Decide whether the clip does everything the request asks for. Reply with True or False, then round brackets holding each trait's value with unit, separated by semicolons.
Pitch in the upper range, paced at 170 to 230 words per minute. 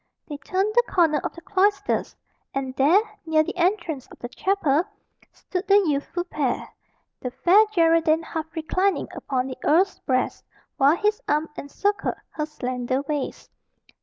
False (320 Hz; 150 wpm)